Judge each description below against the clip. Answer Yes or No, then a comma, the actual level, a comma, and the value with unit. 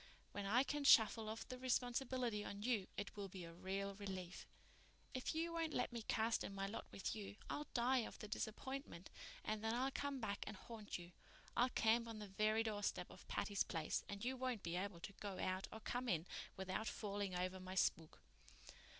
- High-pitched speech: Yes, high, 215 Hz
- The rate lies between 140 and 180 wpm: No, average, 200 wpm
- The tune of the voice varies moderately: Yes, average, 3.9 semitones